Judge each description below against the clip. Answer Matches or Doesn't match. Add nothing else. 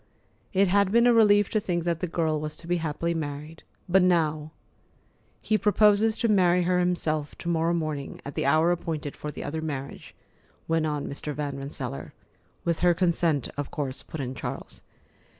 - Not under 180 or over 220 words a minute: Matches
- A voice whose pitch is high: Doesn't match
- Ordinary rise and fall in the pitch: Matches